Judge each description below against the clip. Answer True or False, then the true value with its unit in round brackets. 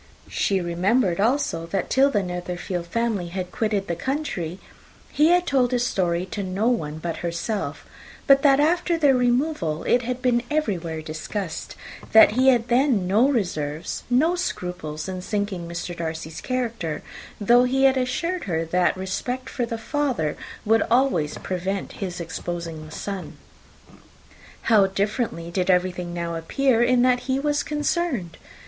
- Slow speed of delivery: False (155 wpm)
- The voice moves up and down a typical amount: False (6.6 semitones)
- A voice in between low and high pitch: False (205 Hz)